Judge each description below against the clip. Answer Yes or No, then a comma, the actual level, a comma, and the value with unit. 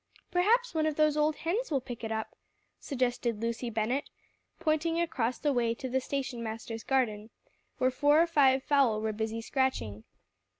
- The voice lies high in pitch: Yes, very high, 260 Hz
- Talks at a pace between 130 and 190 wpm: Yes, average, 170 wpm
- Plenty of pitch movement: No, average, 5.0 semitones